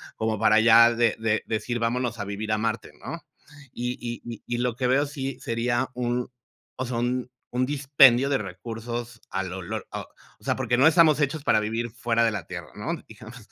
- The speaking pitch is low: Yes, low, 120 Hz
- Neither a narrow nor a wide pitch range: No, narrow, 2.3 semitones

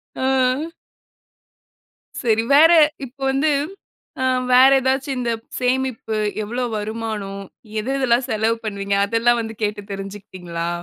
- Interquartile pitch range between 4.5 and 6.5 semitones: No, average, 3.9 semitones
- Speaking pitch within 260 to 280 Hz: No, high, 230 Hz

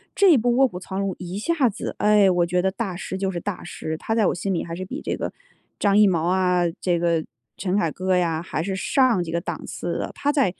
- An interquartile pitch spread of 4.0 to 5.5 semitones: No, average, 3.2 semitones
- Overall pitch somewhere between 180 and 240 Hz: Yes, high, 190 Hz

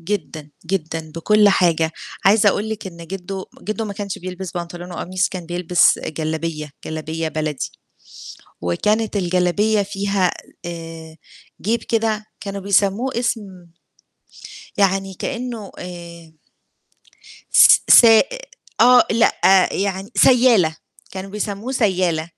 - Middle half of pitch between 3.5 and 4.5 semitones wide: Yes, average, 3.8 semitones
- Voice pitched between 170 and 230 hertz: Yes, high, 190 Hz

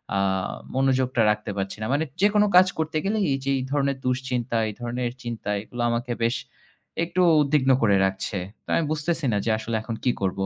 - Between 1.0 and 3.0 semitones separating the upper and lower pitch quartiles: No, average, 4.5 semitones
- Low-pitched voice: Yes, low, 125 Hz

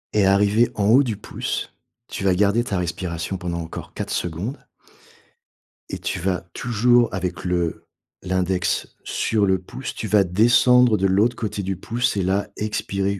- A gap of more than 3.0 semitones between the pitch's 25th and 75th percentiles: Yes, average, 3.4 semitones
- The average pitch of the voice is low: Yes, low, 100 Hz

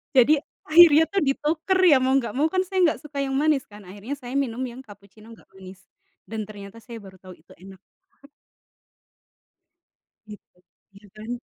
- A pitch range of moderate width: No, wide, 6.3 semitones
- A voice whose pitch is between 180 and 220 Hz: No, high, 245 Hz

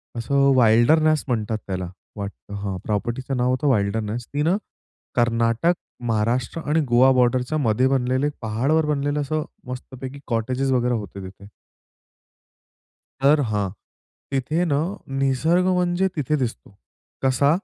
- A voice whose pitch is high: No, low, 130 Hz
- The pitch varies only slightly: No, average, 4.1 semitones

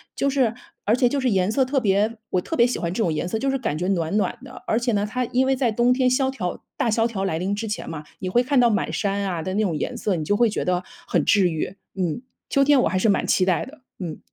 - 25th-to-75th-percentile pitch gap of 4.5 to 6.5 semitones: Yes, wide, 5.4 semitones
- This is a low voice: No, high, 215 Hz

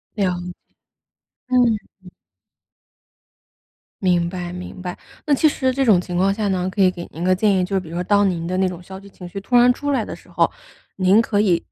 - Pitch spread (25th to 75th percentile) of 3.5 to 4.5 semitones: No, average, 2.8 semitones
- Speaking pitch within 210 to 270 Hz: No, medium, 185 Hz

